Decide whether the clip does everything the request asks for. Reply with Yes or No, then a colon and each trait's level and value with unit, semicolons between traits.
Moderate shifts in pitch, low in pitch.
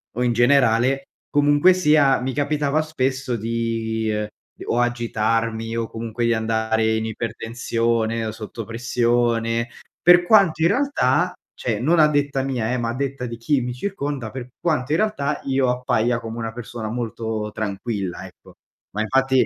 Yes: average, 3.5 semitones; low, 120 Hz